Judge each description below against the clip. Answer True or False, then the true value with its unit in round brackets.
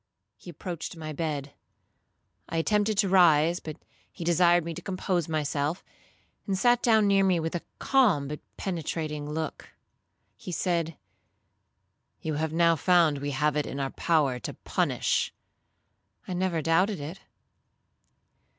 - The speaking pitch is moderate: True (165 Hz)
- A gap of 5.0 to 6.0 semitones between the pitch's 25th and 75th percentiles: False (3.4 semitones)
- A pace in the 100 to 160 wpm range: True (140 wpm)